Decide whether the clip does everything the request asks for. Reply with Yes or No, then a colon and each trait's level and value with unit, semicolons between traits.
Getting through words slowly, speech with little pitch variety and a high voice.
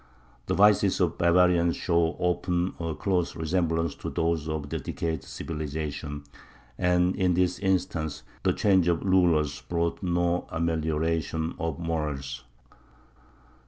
No: slow, 120 wpm; narrow, 2.0 semitones; very low, 85 Hz